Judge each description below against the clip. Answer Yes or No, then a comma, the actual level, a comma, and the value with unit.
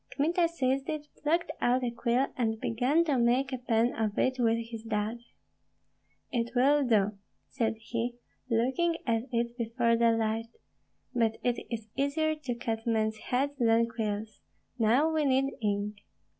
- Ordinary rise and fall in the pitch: Yes, average, 3.0 semitones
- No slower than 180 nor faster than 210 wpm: No, average, 155 wpm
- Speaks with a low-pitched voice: No, high, 235 Hz